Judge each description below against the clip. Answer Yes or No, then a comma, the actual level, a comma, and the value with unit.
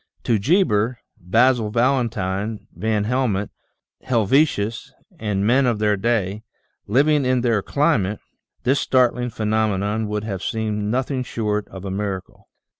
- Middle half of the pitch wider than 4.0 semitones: No, average, 3.5 semitones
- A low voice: Yes, low, 110 Hz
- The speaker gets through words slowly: Yes, slow, 125 wpm